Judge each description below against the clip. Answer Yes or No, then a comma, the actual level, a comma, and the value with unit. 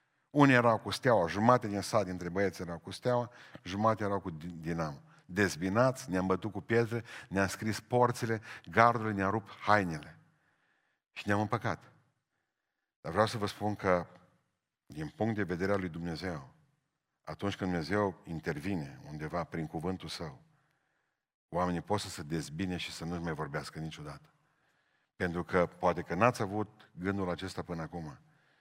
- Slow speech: No, average, 155 wpm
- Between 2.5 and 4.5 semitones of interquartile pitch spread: Yes, average, 4.2 semitones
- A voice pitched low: Yes, very low, 95 Hz